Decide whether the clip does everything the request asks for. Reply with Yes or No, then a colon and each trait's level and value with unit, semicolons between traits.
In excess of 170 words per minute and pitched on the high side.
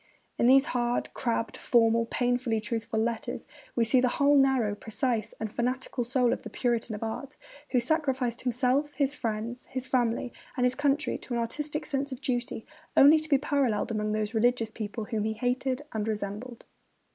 Yes: average, 180 wpm; high, 245 Hz